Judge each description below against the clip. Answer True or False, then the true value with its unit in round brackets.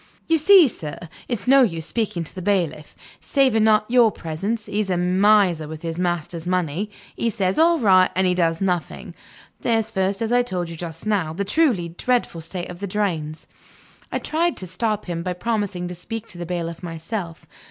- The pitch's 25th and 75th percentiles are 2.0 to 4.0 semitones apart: False (4.6 semitones)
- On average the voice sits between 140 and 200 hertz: True (185 Hz)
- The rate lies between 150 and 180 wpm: False (195 wpm)